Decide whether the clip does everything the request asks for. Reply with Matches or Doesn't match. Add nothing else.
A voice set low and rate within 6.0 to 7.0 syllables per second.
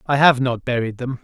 Doesn't match